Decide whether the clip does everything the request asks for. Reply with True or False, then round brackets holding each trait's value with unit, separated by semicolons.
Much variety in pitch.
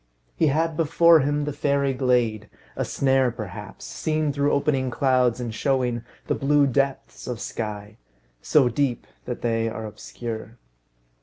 False (3.8 semitones)